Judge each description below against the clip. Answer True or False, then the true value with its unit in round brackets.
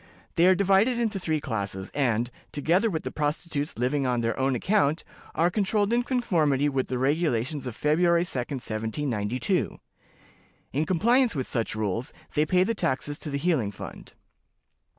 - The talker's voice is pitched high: False (145 Hz)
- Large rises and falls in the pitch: True (6.4 semitones)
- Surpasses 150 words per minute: True (160 wpm)